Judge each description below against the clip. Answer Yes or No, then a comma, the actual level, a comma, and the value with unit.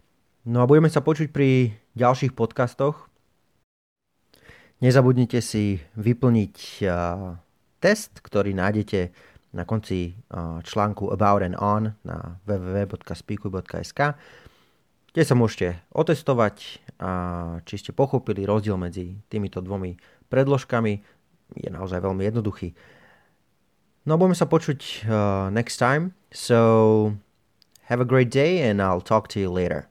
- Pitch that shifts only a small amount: No, average, 5.0 semitones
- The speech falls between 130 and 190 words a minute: No, average, 120 wpm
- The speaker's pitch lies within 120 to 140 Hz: No, low, 105 Hz